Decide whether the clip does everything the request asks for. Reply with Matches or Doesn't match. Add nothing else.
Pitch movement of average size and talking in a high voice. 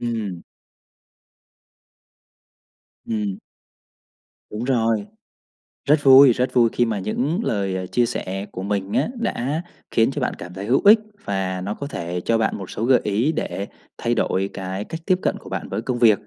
Doesn't match